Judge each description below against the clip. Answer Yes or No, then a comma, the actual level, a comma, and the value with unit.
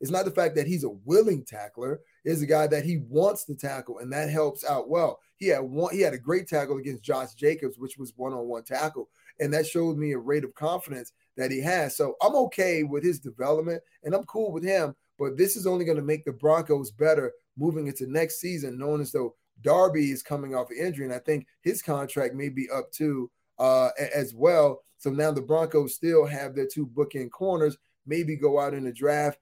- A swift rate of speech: Yes, fast, 230 wpm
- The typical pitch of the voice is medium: Yes, medium, 150 Hz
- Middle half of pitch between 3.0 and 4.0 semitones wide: Yes, average, 3.4 semitones